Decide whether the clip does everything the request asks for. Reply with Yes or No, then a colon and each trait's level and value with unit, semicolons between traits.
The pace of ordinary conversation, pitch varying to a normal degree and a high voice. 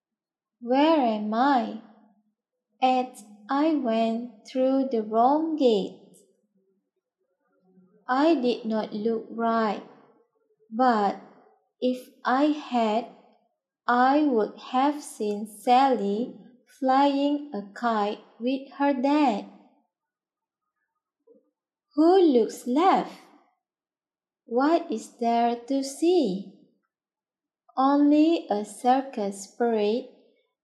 No: slow, 80 wpm; average, 4.2 semitones; high, 245 Hz